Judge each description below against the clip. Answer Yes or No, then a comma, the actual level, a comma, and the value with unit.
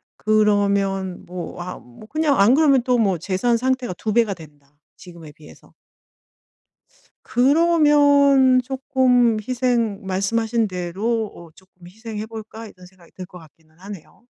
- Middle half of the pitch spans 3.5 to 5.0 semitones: No, wide, 5.4 semitones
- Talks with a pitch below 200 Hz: No, high, 215 Hz